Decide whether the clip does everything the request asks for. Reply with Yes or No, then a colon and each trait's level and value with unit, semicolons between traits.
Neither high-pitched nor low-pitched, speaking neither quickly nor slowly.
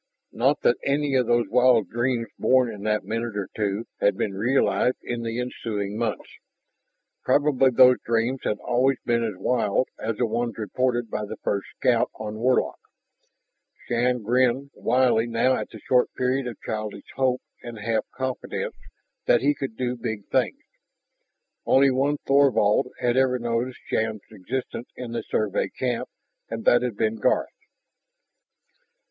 No: low, 120 Hz; average, 155 wpm